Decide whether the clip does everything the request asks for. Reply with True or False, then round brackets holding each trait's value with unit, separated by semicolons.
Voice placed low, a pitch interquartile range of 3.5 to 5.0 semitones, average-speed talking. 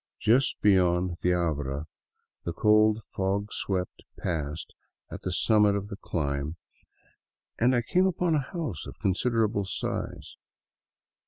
False (100 Hz; 4.4 semitones; 120 wpm)